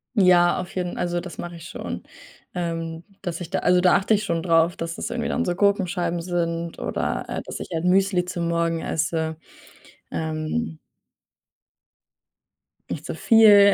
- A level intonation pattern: Yes, narrow, 1.8 semitones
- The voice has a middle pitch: Yes, medium, 175 Hz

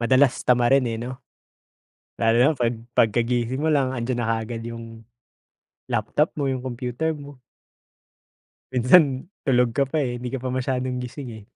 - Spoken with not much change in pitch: Yes, narrow, 2.2 semitones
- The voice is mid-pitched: No, low, 125 Hz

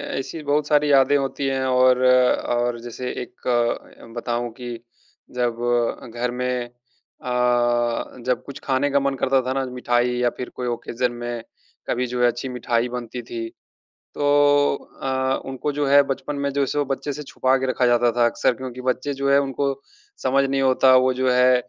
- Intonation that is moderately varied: No, narrow, 1.9 semitones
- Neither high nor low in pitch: No, low, 125 Hz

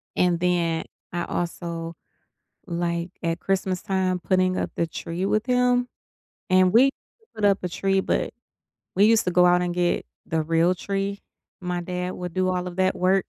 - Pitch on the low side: No, medium, 180 Hz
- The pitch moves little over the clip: Yes, narrow, 1.9 semitones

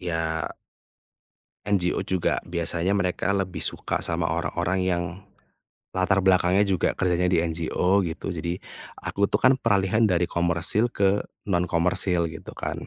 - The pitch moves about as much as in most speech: No, narrow, 2.1 semitones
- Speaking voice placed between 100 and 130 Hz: No, very low, 90 Hz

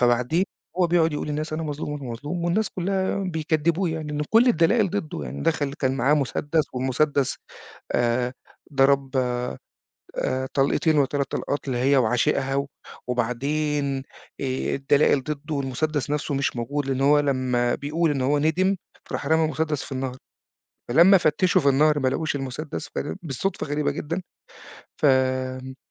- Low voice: No, medium, 145 Hz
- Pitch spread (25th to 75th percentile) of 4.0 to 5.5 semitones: No, average, 3.1 semitones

